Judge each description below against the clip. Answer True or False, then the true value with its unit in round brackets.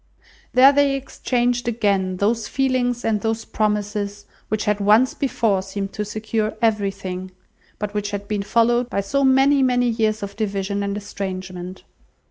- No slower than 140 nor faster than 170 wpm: True (150 wpm)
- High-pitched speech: True (210 Hz)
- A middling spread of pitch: True (3.1 semitones)